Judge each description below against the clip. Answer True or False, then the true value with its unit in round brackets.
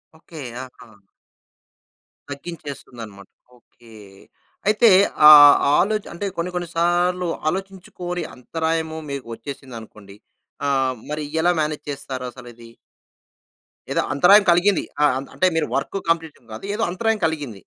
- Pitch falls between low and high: True (160 Hz)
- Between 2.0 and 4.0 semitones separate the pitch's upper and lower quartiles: False (5.4 semitones)